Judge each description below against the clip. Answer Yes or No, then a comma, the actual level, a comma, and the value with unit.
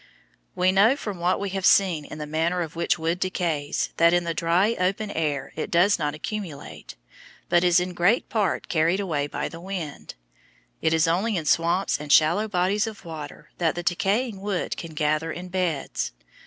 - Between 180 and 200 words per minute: Yes, average, 190 wpm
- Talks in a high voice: No, medium, 175 Hz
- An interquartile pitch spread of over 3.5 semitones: No, average, 3.2 semitones